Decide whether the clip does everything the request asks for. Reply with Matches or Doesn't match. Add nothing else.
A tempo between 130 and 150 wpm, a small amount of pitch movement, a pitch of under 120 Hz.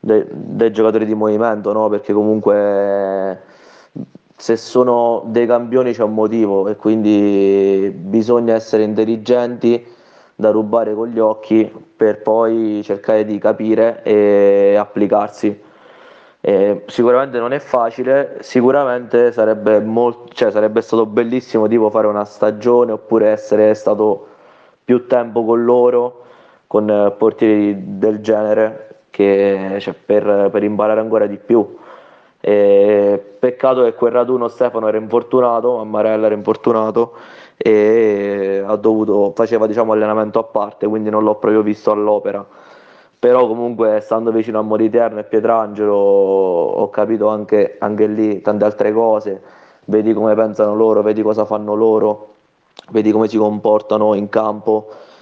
Matches